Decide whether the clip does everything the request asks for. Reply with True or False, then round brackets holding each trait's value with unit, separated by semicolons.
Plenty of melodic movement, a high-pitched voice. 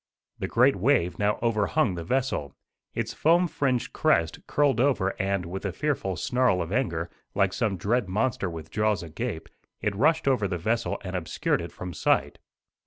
False (5.9 semitones; 105 Hz)